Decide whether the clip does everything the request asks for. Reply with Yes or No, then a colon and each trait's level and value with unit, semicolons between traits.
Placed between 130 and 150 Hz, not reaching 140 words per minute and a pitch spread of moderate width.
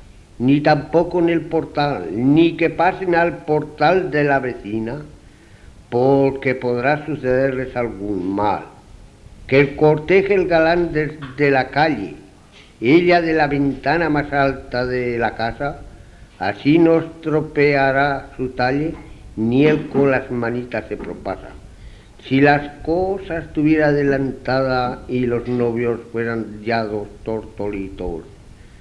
Yes: low, 135 Hz; slow, 125 wpm; average, 4.6 semitones